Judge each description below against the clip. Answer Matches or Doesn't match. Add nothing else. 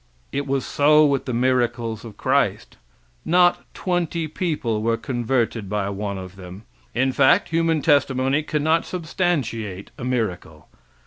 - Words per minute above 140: Doesn't match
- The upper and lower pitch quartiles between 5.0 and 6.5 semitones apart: Matches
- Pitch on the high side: Doesn't match